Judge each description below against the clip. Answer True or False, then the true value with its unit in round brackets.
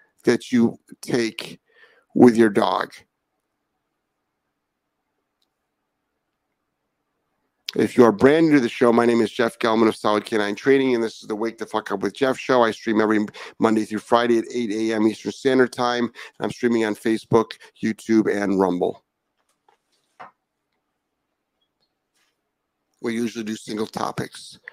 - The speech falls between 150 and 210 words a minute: False (140 wpm)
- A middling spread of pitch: False (1.6 semitones)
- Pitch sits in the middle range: False (115 Hz)